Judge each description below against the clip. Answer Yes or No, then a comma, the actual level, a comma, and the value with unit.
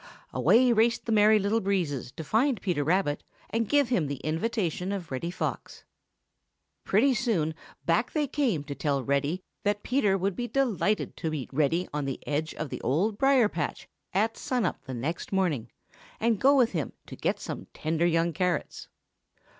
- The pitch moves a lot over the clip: Yes, wide, 6.6 semitones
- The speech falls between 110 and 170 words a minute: No, average, 180 wpm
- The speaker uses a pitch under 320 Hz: Yes, medium, 185 Hz